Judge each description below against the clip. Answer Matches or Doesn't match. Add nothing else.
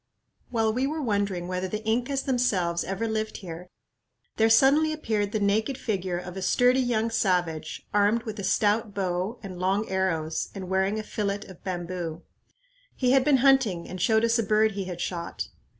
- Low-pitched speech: Doesn't match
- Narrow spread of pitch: Doesn't match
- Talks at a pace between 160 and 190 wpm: Matches